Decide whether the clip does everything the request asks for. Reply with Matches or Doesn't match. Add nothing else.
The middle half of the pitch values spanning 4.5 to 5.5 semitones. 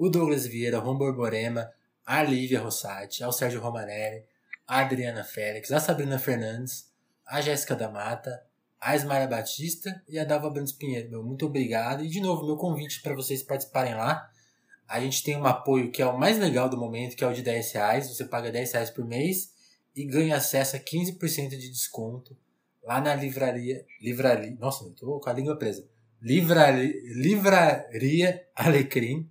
Doesn't match